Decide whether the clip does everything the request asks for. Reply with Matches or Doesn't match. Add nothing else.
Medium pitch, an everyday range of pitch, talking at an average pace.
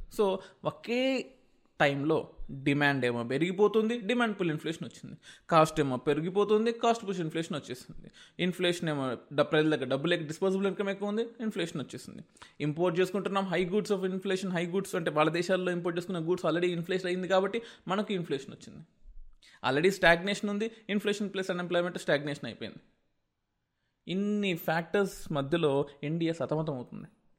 Doesn't match